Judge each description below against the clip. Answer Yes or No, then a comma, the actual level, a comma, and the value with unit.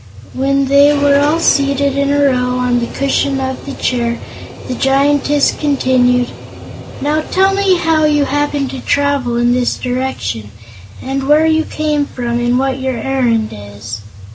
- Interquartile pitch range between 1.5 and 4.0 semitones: Yes, narrow, 2.5 semitones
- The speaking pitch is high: Yes, very high, 270 Hz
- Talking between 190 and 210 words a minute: No, average, 160 wpm